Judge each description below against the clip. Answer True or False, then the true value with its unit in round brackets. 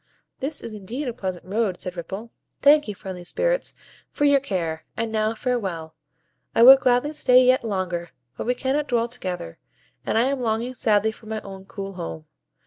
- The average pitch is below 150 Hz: False (220 Hz)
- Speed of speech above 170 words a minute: True (185 wpm)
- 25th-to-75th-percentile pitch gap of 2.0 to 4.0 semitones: False (5.1 semitones)